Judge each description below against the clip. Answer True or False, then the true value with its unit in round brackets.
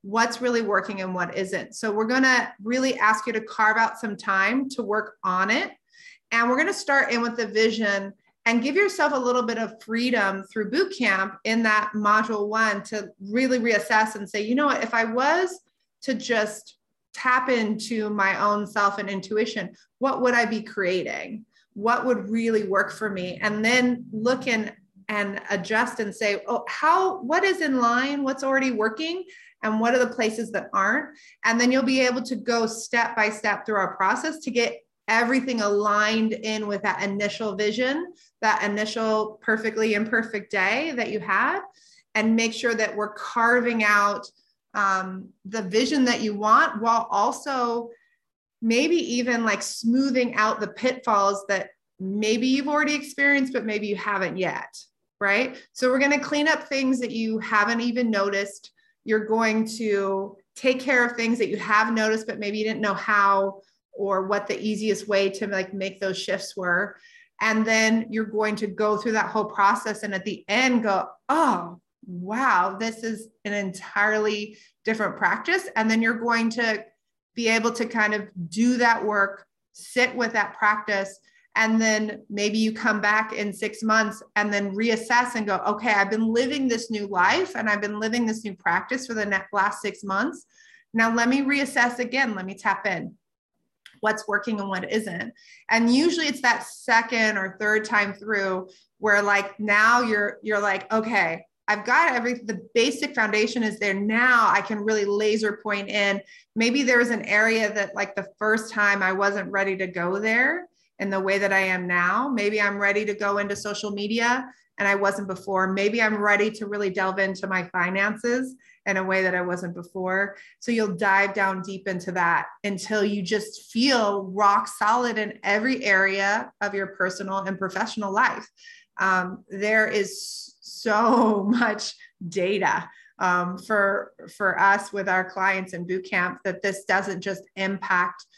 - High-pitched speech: True (215 Hz)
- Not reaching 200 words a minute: True (180 wpm)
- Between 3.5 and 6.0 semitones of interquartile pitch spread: False (2.9 semitones)